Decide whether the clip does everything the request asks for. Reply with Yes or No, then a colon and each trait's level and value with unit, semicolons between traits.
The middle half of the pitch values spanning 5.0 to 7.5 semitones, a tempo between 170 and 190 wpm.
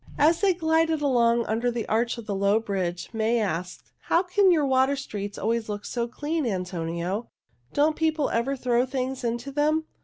Yes: wide, 5.6 semitones; average, 180 wpm